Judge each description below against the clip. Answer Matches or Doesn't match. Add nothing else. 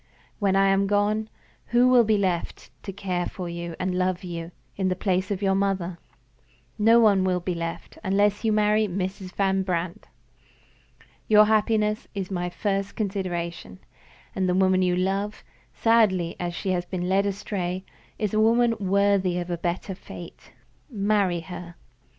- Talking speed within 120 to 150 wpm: Doesn't match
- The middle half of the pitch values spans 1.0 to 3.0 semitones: Matches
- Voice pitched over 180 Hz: Matches